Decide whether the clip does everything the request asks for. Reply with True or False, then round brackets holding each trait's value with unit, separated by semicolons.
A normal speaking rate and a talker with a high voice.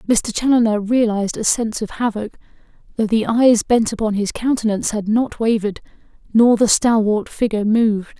True (160 wpm; 220 Hz)